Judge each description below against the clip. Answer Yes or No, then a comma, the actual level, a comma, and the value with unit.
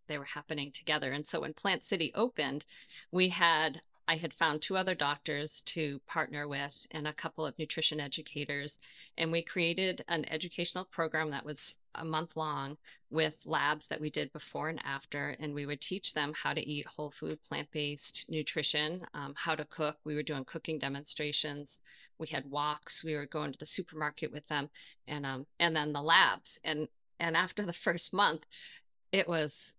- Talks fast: No, average, 185 wpm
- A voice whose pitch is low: No, medium, 155 Hz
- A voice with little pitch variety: Yes, narrow, 2.0 semitones